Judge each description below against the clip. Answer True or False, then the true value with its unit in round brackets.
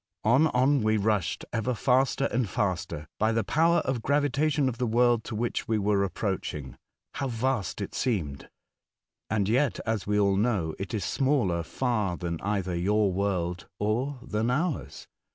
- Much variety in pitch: False (4.6 semitones)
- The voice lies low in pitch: True (110 Hz)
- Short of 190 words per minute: True (180 wpm)